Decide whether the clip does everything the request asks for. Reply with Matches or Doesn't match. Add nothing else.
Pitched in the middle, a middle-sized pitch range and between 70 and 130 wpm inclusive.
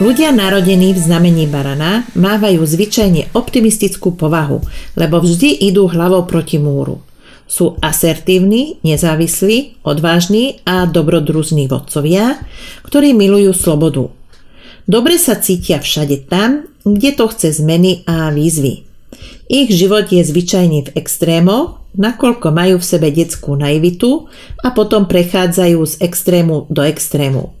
Matches